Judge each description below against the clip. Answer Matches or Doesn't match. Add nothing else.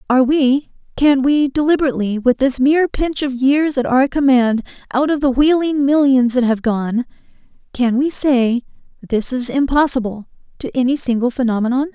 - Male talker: Doesn't match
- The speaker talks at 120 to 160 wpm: Matches